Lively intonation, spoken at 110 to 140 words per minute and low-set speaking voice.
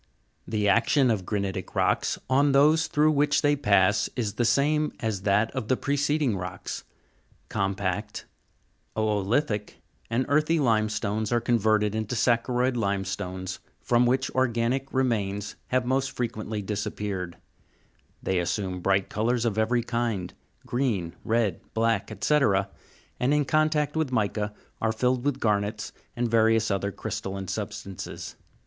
No: average, 4.2 semitones; slow, 135 wpm; low, 115 Hz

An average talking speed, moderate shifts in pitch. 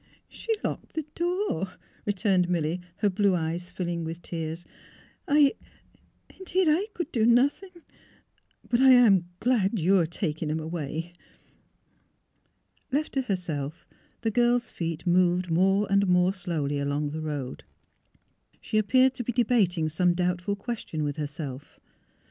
No: average, 145 wpm; wide, 6.7 semitones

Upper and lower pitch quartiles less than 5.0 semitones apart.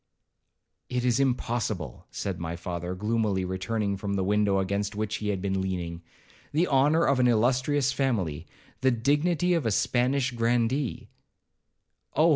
No: wide, 5.4 semitones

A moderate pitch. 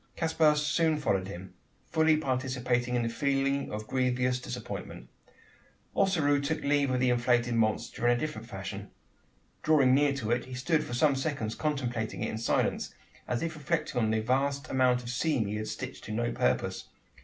No: low, 130 Hz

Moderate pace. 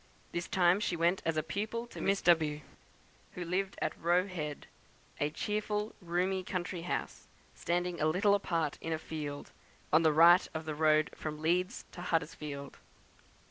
Yes: average, 165 wpm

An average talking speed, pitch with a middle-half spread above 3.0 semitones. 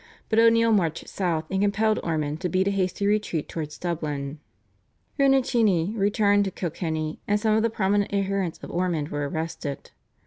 Yes: average, 165 wpm; average, 4.5 semitones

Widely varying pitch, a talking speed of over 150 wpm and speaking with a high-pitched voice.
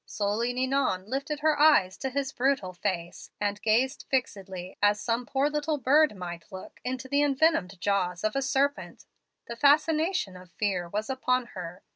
Yes: wide, 6.5 semitones; average, 165 wpm; high, 245 Hz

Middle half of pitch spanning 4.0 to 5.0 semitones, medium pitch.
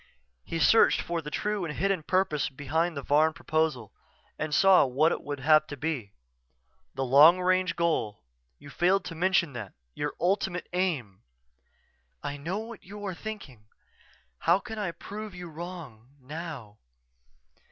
Yes: average, 4.4 semitones; medium, 160 Hz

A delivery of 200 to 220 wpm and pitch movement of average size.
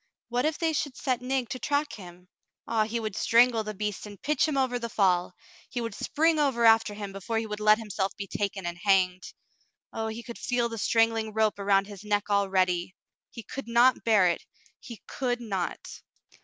Yes: fast, 205 wpm; average, 3.5 semitones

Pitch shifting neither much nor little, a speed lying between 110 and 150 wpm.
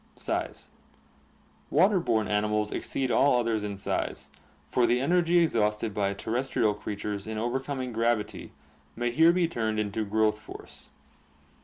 Yes: average, 3.9 semitones; average, 140 wpm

